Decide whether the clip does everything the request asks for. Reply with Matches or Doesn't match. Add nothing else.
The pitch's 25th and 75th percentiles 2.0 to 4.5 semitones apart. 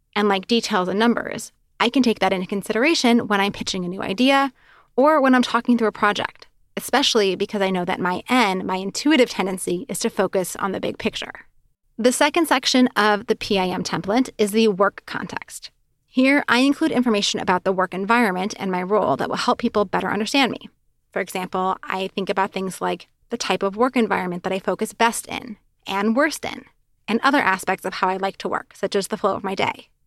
Matches